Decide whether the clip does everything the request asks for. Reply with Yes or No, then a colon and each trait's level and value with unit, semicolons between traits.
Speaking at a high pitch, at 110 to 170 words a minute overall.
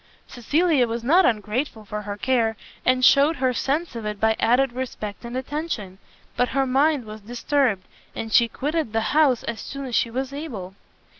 No: high, 245 Hz; average, 180 wpm